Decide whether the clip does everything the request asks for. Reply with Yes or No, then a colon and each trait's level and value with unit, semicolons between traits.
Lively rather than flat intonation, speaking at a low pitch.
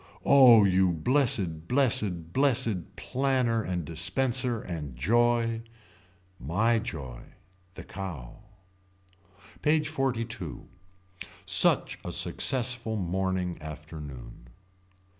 Yes: wide, 6.5 semitones; low, 100 Hz